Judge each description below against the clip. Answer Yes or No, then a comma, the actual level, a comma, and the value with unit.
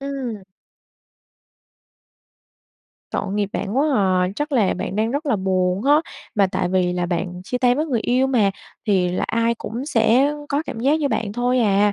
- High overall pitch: Yes, high, 225 Hz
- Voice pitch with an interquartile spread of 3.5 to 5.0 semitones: No, wide, 5.4 semitones